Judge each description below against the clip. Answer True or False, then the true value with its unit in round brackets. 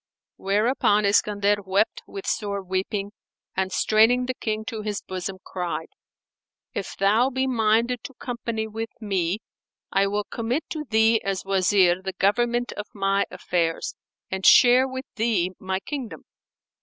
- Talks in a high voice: True (210 Hz)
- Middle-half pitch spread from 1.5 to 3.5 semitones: True (3.2 semitones)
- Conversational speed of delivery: True (145 wpm)